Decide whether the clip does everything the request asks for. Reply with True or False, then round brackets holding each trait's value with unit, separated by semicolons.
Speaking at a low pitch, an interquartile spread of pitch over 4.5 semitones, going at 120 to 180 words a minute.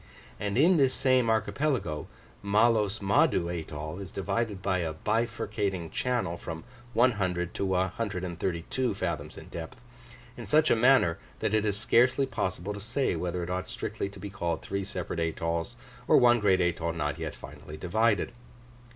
True (100 Hz; 5.1 semitones; 160 wpm)